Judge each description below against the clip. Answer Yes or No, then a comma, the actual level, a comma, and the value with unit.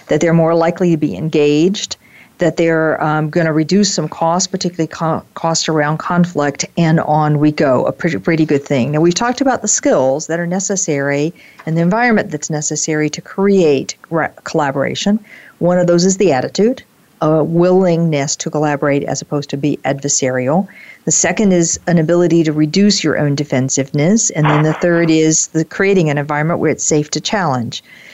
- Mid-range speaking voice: Yes, medium, 160 Hz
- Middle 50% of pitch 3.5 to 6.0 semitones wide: No, average, 2.8 semitones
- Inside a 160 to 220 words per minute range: Yes, average, 180 wpm